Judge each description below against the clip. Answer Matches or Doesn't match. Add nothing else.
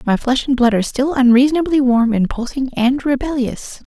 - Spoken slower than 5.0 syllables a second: Doesn't match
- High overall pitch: Matches